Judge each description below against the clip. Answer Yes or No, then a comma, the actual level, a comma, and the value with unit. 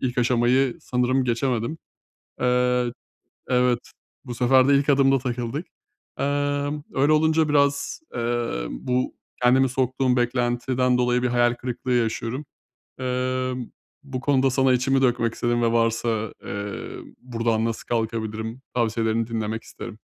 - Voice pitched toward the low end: Yes, low, 125 Hz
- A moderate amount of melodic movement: No, narrow, 2.1 semitones